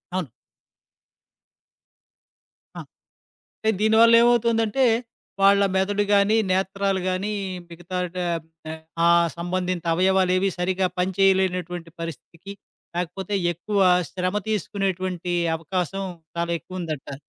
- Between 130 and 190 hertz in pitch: Yes, medium, 185 Hz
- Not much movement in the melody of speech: Yes, narrow, 2.2 semitones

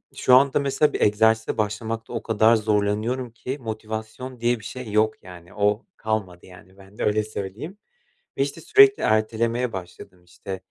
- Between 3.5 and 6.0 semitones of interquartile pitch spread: No, narrow, 2.6 semitones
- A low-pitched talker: Yes, low, 110 Hz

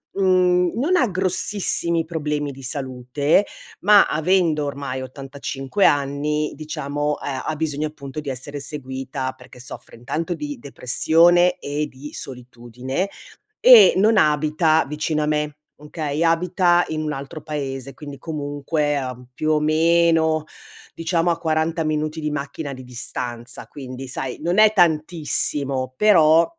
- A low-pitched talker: No, medium, 150 Hz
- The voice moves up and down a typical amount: Yes, average, 3.3 semitones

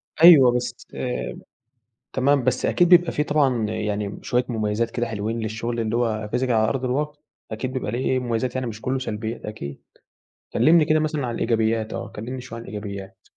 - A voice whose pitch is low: Yes, low, 120 Hz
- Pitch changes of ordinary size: Yes, average, 3.0 semitones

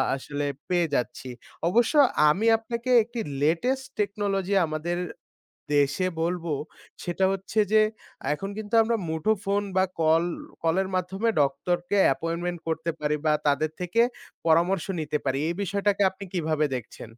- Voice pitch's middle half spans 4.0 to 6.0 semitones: Yes, average, 4.4 semitones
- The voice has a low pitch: No, medium, 175 Hz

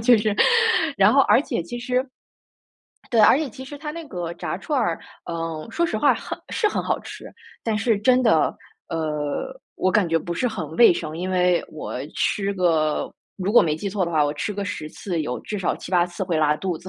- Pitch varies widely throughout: Yes, wide, 6.0 semitones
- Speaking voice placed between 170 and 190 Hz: Yes, medium, 185 Hz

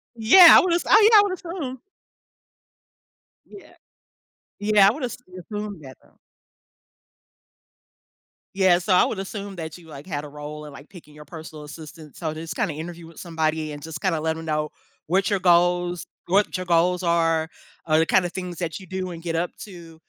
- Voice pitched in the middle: Yes, medium, 170 Hz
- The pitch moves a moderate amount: Yes, average, 3.4 semitones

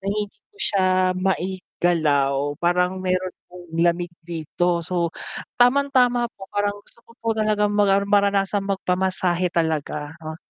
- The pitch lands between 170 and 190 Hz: Yes, medium, 185 Hz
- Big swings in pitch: No, average, 3.0 semitones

